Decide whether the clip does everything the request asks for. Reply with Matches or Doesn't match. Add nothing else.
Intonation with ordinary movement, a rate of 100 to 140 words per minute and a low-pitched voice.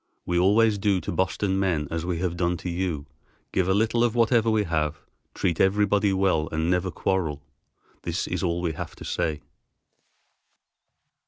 Doesn't match